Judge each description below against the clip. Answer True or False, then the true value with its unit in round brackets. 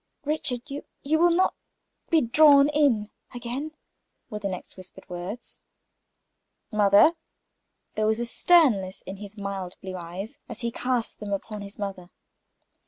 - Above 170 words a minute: False (145 wpm)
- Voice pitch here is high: True (220 Hz)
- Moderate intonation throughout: False (6.1 semitones)